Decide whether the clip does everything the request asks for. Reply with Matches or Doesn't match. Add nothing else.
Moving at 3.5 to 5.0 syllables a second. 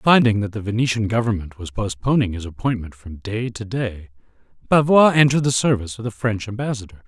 Doesn't match